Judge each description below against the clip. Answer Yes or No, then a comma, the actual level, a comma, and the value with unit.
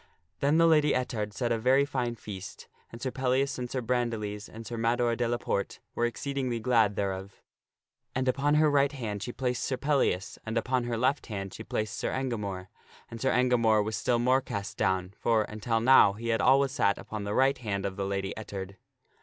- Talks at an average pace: No, fast, 210 wpm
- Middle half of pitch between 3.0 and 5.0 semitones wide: Yes, average, 3.9 semitones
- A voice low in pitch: Yes, low, 115 Hz